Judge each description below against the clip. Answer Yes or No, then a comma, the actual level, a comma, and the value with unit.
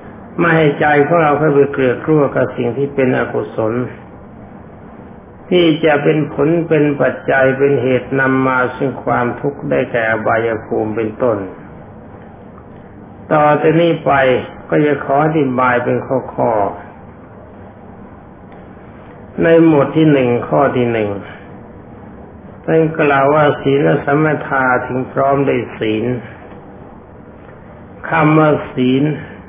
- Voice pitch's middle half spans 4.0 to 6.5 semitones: No, average, 3.4 semitones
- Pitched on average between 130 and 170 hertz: Yes, low, 135 Hz